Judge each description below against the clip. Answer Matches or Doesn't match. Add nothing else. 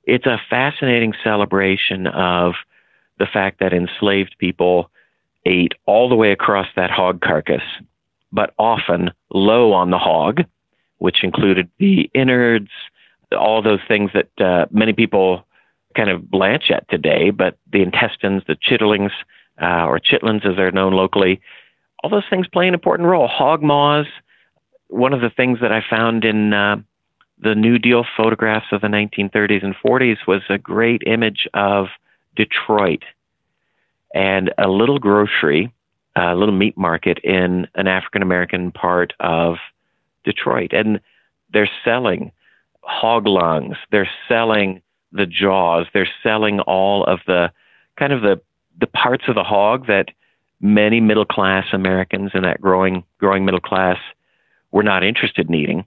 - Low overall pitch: Matches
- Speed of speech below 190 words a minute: Matches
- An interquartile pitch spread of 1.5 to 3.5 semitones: Matches